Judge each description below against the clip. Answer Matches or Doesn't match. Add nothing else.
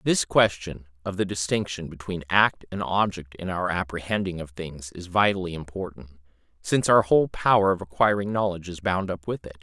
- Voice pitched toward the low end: Matches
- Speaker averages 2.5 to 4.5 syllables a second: Doesn't match